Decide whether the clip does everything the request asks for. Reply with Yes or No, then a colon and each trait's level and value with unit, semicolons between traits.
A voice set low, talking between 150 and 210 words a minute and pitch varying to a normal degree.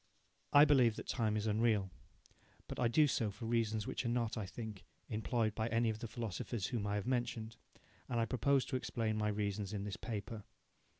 No: low, 110 Hz; average, 200 wpm; narrow, 2.0 semitones